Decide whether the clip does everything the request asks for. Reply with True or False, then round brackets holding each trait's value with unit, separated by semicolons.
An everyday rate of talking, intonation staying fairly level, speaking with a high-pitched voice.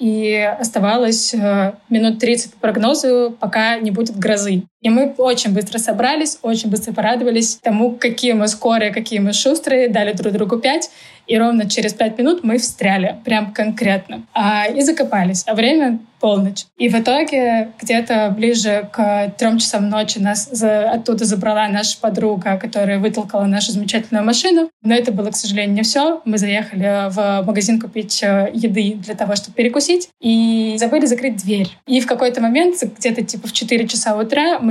False (165 wpm; 2.2 semitones; 225 Hz)